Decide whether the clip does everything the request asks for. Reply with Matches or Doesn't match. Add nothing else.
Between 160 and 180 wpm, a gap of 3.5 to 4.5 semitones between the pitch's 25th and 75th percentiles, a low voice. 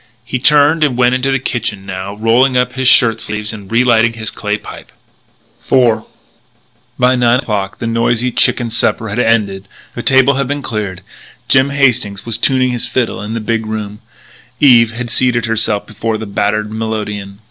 Doesn't match